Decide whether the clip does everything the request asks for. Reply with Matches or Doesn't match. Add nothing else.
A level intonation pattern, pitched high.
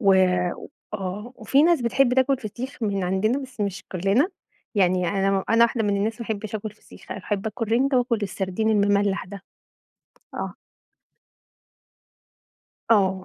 Doesn't match